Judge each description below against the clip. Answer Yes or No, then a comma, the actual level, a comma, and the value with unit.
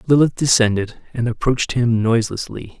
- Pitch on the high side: No, low, 120 Hz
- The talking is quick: No, slow, 130 wpm